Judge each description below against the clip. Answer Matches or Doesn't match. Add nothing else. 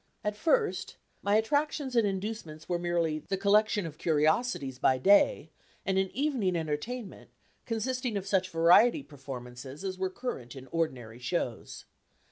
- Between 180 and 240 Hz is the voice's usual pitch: Matches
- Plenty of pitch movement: Matches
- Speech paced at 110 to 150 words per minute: Matches